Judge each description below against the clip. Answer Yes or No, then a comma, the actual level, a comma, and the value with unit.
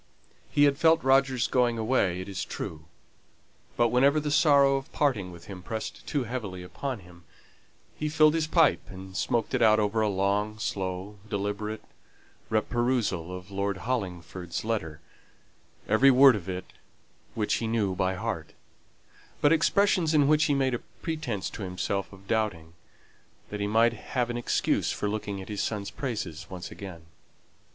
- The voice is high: No, low, 110 Hz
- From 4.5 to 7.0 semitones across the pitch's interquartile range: Yes, wide, 5.6 semitones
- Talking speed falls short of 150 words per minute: No, average, 160 wpm